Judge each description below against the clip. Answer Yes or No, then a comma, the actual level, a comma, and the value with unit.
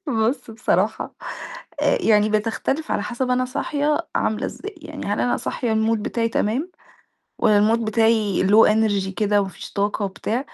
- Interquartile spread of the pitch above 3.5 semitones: No, average, 3.2 semitones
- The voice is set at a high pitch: Yes, high, 225 Hz